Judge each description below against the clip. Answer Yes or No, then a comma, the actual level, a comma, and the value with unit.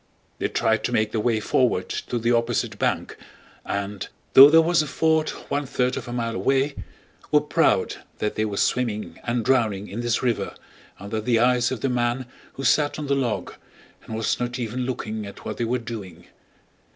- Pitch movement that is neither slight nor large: Yes, average, 3.0 semitones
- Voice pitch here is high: No, low, 120 Hz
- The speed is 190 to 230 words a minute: Yes, average, 195 wpm